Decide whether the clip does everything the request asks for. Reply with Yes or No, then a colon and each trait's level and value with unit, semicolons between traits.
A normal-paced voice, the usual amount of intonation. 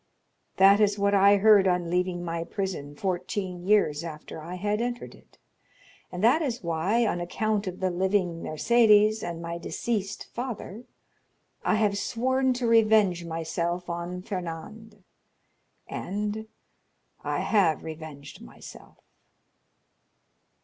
No: slow, 120 wpm; average, 3.9 semitones